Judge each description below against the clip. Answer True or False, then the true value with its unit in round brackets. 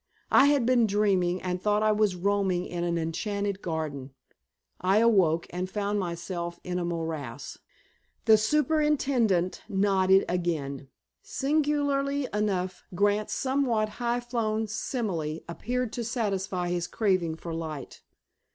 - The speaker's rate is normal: False (125 wpm)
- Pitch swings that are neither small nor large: True (4.7 semitones)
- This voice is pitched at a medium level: False (195 Hz)